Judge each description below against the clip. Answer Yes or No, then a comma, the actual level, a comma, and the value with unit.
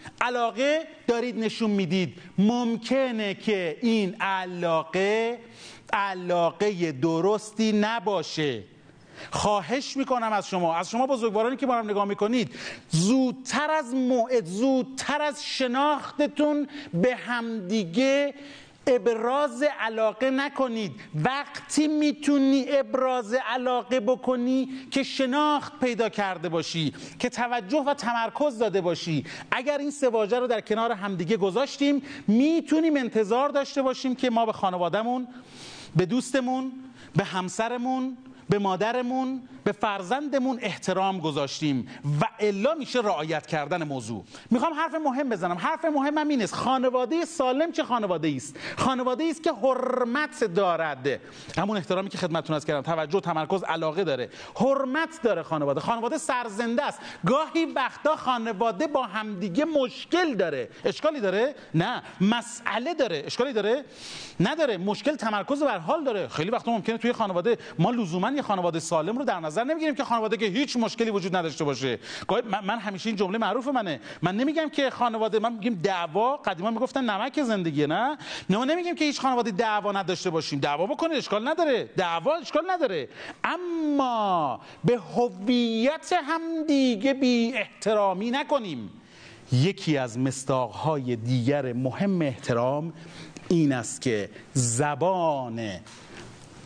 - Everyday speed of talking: Yes, average, 130 wpm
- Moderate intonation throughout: No, wide, 6.3 semitones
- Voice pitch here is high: Yes, high, 230 Hz